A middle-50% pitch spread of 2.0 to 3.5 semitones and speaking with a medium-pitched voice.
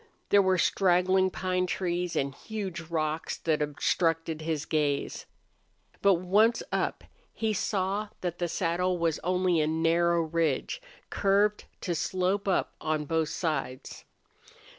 Yes: average, 2.9 semitones; medium, 175 Hz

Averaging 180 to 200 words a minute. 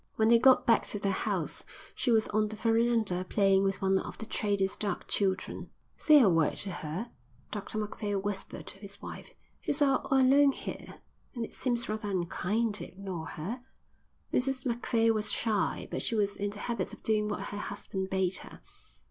Yes: average, 190 wpm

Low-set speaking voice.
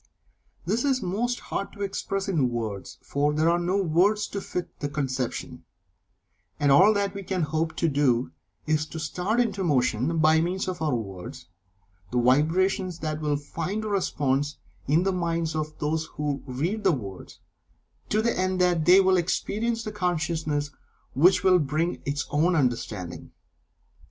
No: medium, 160 Hz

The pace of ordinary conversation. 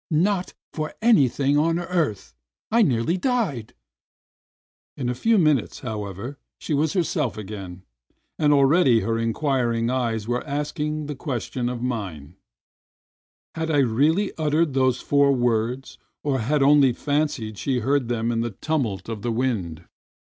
Yes: average, 145 wpm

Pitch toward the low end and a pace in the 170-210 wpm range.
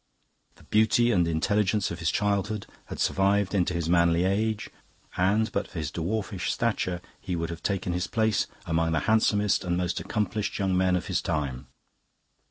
Yes: very low, 95 Hz; average, 175 wpm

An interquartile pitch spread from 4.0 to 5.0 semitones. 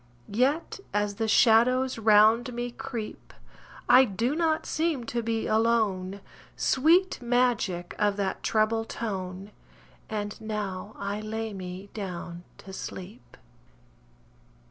No: average, 3.4 semitones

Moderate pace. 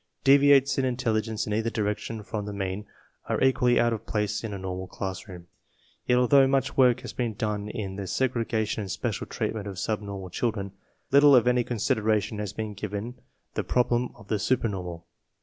Yes: average, 185 wpm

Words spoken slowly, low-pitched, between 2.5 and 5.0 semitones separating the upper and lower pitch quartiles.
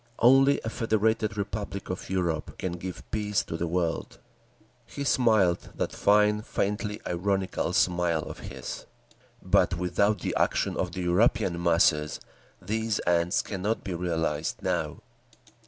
Yes: slow, 125 wpm; very low, 95 Hz; average, 3.5 semitones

